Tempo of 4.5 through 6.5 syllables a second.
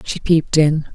Yes: 4.9 syllables/s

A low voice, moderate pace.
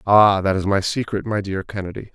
No: low, 100 Hz; fast, 225 wpm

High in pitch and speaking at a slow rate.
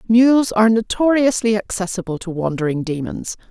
Yes: high, 210 Hz; slow, 120 wpm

